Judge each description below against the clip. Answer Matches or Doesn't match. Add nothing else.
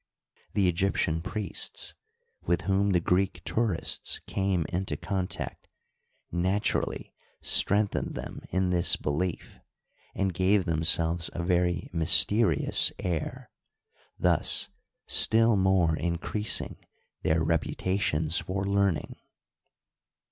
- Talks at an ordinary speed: Doesn't match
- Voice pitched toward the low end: Matches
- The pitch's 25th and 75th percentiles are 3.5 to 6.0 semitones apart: Doesn't match